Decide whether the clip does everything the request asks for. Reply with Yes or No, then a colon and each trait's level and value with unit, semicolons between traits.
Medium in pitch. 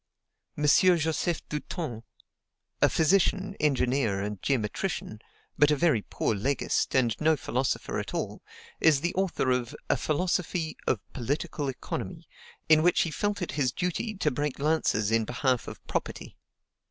Yes: medium, 150 Hz